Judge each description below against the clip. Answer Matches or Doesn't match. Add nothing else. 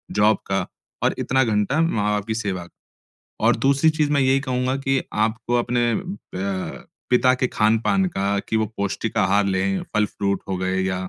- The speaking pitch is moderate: Doesn't match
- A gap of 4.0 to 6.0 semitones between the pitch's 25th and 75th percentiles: Matches